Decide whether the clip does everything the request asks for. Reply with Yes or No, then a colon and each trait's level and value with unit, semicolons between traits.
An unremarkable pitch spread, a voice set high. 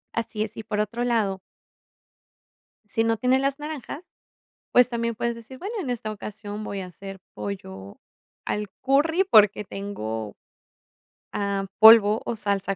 Yes: average, 3.3 semitones; high, 215 Hz